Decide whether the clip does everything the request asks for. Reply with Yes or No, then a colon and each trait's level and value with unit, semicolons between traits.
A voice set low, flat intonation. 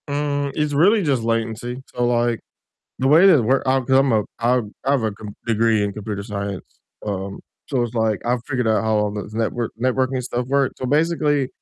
No: low, 120 Hz; average, 3.8 semitones